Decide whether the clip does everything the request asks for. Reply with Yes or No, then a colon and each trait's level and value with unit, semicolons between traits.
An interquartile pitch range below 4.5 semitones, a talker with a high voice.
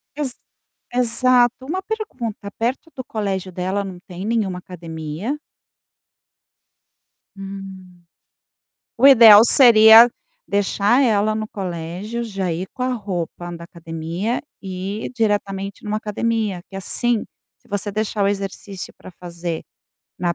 Yes: average, 4.0 semitones; high, 205 Hz